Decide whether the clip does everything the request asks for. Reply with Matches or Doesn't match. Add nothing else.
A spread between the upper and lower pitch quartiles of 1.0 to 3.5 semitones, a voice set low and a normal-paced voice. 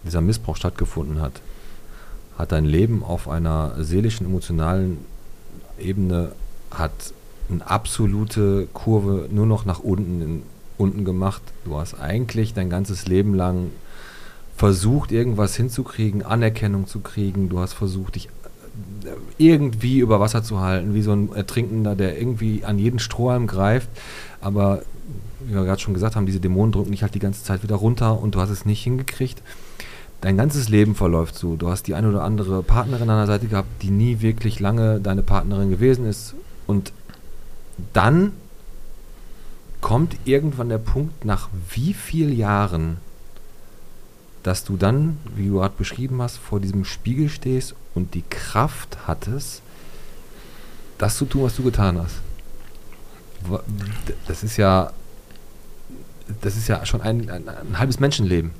Matches